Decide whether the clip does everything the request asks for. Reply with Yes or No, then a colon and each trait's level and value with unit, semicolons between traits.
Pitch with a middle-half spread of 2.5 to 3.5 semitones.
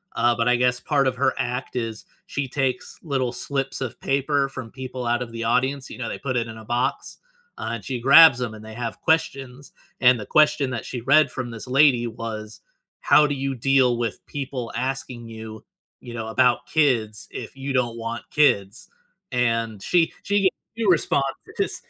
Yes: average, 2.9 semitones